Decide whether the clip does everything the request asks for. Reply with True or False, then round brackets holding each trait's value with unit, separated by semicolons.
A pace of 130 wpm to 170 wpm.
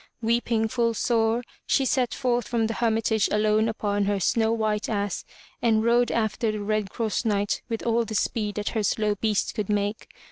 False (185 wpm)